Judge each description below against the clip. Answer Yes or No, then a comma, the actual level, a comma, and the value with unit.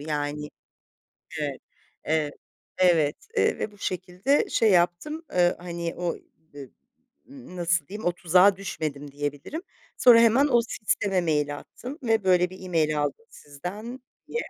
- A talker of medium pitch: Yes, medium, 180 Hz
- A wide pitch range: Yes, wide, 5.7 semitones